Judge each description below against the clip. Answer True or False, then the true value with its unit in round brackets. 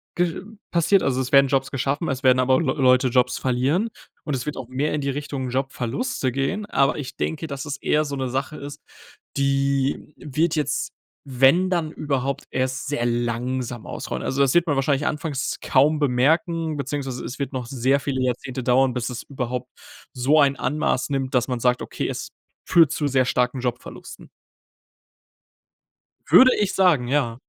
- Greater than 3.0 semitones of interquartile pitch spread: False (2.7 semitones)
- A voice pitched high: False (135 Hz)